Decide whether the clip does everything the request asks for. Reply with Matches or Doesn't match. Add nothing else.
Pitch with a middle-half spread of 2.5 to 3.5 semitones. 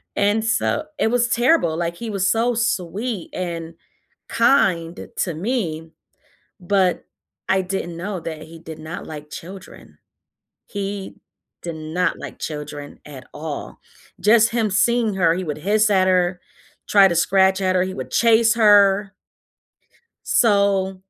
Doesn't match